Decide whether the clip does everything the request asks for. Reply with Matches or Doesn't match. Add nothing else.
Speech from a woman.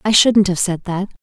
Matches